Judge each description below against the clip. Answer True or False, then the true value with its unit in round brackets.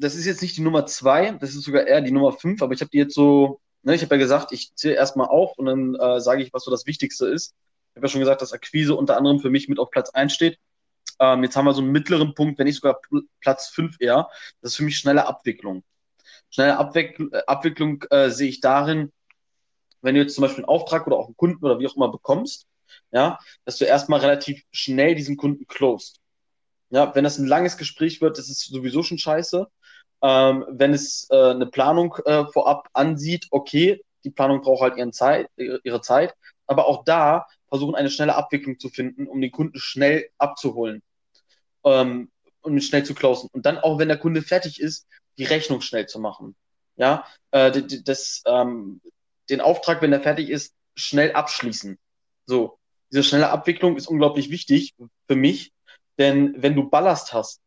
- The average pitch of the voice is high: False (140 Hz)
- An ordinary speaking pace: False (205 wpm)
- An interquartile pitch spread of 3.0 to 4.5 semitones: False (2.6 semitones)